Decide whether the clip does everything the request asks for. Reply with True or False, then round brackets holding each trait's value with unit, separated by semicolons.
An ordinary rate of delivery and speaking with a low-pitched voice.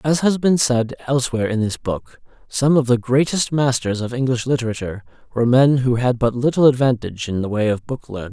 False (210 wpm; 125 Hz)